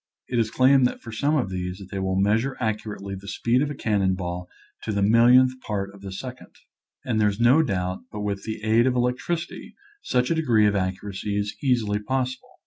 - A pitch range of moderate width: Yes, average, 4.2 semitones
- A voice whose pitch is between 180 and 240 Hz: No, low, 110 Hz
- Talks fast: Yes, fast, 215 wpm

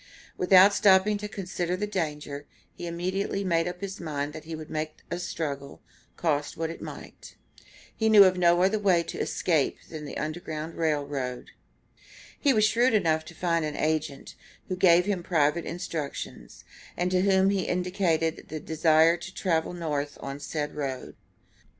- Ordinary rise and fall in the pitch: Yes, average, 3.3 semitones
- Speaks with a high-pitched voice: No, medium, 170 Hz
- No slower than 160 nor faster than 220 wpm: Yes, average, 170 wpm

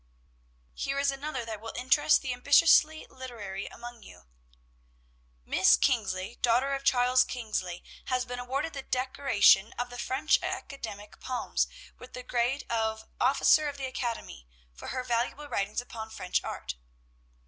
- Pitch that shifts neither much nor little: Yes, average, 3.4 semitones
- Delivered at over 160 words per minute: No, average, 145 wpm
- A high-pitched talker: Yes, high, 245 Hz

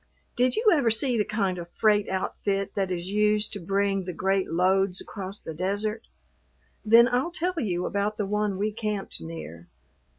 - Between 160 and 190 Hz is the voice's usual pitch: No, high, 200 Hz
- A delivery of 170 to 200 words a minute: Yes, average, 175 wpm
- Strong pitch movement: No, narrow, 2.6 semitones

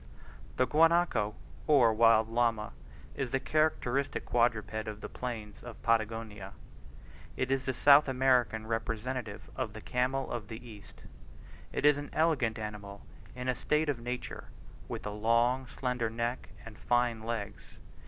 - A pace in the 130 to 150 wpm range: Yes, average, 145 wpm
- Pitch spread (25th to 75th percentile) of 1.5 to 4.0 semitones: Yes, average, 2.9 semitones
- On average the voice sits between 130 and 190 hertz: No, low, 120 Hz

